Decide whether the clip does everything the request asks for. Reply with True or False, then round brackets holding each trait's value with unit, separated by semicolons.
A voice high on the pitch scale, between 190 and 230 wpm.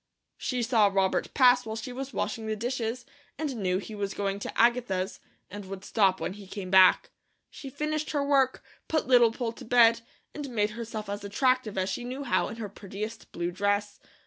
True (225 Hz; 200 wpm)